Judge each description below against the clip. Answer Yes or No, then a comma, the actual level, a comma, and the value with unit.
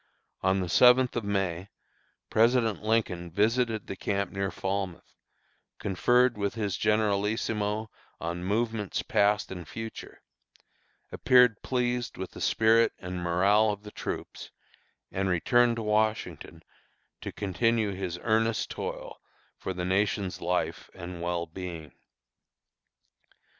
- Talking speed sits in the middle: No, slow, 120 wpm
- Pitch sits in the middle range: No, low, 100 Hz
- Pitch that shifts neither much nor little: Yes, average, 3.5 semitones